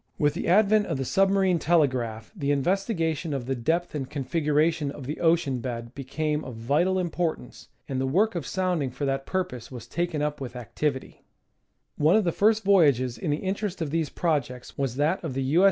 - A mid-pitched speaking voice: Yes, medium, 150 Hz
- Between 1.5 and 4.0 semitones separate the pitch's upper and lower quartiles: No, average, 4.7 semitones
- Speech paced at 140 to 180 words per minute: No, average, 195 wpm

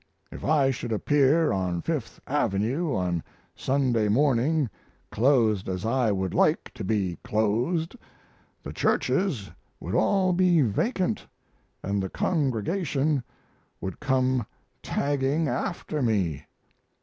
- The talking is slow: Yes, slow, 115 wpm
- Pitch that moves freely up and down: Yes, wide, 6.6 semitones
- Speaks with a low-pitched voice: Yes, low, 130 Hz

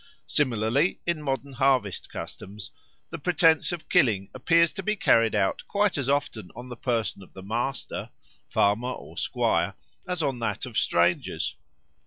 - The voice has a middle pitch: No, low, 130 Hz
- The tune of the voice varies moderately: No, wide, 6.3 semitones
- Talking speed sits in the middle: Yes, average, 155 wpm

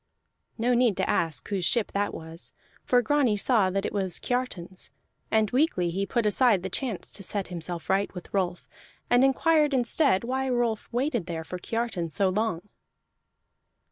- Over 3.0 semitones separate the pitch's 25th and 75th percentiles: Yes, average, 5.2 semitones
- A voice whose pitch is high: Yes, high, 210 Hz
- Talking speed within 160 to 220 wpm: Yes, average, 170 wpm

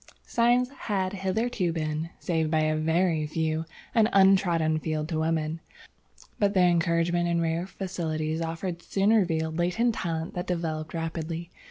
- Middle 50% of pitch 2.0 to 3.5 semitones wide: Yes, average, 2.9 semitones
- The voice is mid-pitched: Yes, medium, 170 Hz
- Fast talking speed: No, average, 145 wpm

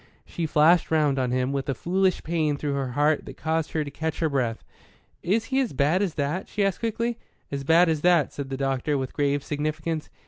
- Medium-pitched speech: Yes, medium, 155 Hz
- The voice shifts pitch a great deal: No, average, 3.5 semitones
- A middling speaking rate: No, fast, 220 wpm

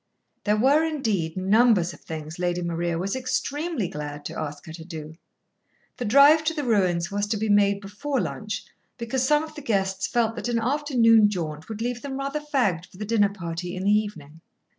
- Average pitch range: No, wide, 6.5 semitones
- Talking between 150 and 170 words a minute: No, average, 200 wpm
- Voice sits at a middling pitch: No, high, 205 Hz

